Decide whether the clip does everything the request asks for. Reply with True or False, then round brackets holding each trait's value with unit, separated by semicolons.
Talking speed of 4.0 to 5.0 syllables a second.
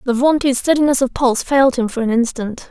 False (6.2 syllables/s)